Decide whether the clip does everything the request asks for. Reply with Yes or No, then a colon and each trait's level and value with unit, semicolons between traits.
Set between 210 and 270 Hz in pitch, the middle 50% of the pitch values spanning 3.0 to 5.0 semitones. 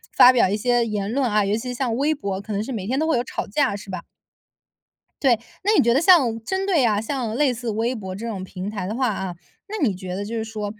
Yes: high, 225 Hz; average, 4.0 semitones